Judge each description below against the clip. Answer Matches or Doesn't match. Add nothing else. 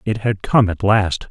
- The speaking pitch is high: Doesn't match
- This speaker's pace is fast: Matches